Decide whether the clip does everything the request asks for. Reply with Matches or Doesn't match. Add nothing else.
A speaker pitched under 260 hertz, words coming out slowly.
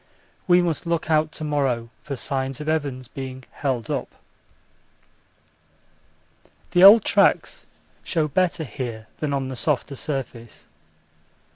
Matches